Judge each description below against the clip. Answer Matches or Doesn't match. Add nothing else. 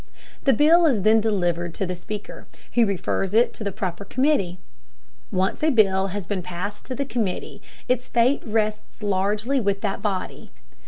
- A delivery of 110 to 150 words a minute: Doesn't match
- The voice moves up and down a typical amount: Matches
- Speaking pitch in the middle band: Doesn't match